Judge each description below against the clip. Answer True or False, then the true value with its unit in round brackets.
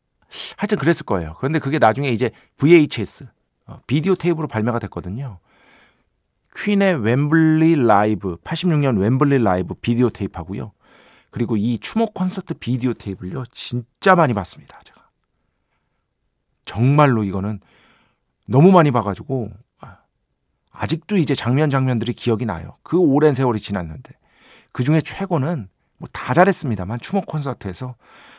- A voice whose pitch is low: True (125 Hz)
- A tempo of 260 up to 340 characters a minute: True (315 characters per minute)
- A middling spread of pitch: False (6.8 semitones)